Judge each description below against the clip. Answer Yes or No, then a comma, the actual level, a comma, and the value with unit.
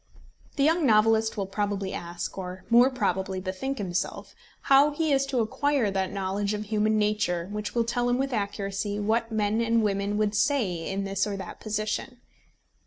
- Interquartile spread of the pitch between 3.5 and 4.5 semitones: No, average, 3.1 semitones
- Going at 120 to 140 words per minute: No, average, 175 wpm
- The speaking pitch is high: Yes, high, 210 Hz